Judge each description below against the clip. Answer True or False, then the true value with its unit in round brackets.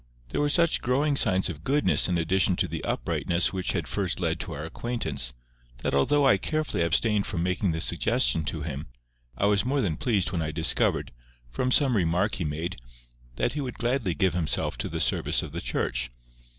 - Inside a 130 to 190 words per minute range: False (200 wpm)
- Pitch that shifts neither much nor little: False (7.0 semitones)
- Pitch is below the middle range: True (95 Hz)